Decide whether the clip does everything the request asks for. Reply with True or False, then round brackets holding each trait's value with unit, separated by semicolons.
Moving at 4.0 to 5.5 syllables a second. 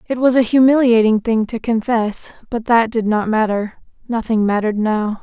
True (5.0 syllables/s)